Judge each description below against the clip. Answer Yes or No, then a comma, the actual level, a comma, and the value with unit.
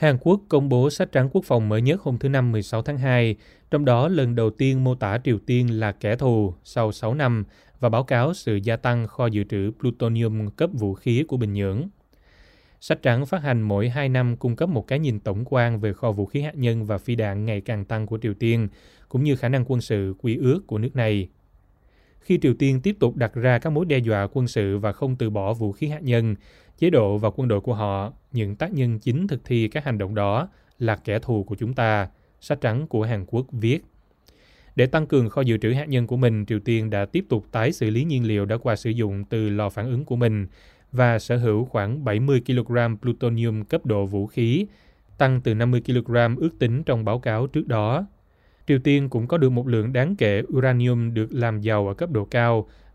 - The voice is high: No, low, 120 Hz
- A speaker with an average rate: Yes, average, 235 wpm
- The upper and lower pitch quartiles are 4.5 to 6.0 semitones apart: No, average, 3.3 semitones